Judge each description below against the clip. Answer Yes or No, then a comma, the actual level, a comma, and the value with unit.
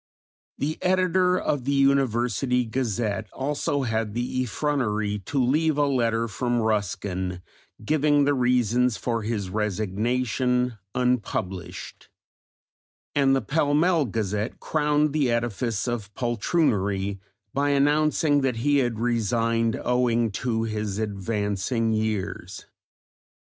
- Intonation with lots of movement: No, average, 4.4 semitones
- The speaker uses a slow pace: Yes, slow, 110 wpm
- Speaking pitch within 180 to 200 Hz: No, low, 120 Hz